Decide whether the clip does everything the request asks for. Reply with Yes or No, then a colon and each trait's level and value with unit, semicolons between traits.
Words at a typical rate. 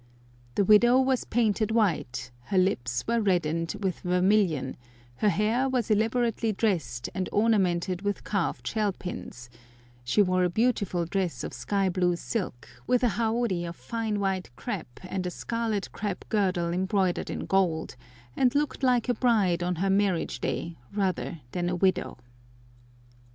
Yes: average, 150 wpm